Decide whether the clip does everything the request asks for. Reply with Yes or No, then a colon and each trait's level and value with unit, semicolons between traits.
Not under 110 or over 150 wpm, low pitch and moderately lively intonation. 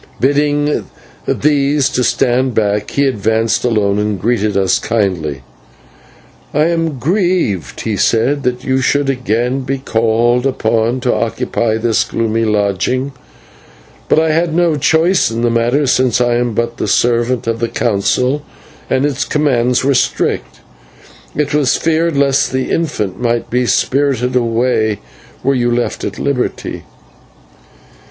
Yes: average, 140 wpm; low, 125 Hz; average, 3.7 semitones